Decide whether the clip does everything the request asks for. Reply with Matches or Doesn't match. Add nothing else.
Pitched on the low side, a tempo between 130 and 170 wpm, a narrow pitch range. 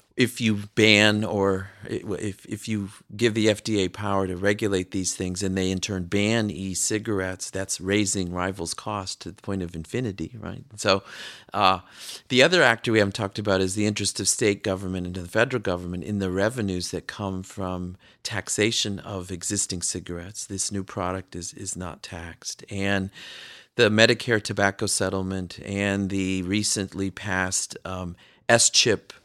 Matches